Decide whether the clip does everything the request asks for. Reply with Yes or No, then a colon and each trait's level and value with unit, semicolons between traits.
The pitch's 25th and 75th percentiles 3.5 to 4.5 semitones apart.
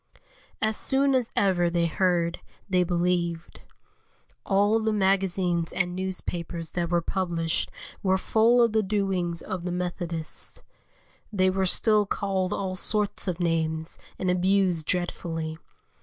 No: narrow, 2.4 semitones